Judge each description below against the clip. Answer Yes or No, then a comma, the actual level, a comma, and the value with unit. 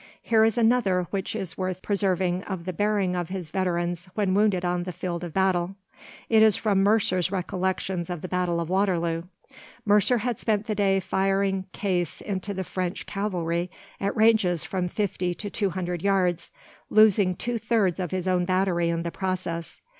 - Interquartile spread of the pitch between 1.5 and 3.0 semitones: Yes, narrow, 2.4 semitones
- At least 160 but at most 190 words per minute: Yes, average, 175 wpm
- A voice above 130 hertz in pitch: Yes, medium, 185 Hz